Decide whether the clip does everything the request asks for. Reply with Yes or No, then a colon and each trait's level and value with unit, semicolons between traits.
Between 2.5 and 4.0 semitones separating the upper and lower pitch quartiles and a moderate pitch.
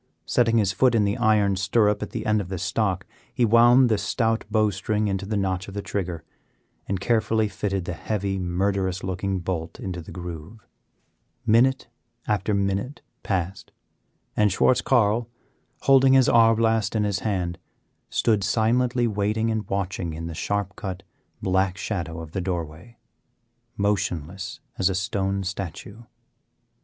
No: average, 2.9 semitones; low, 100 Hz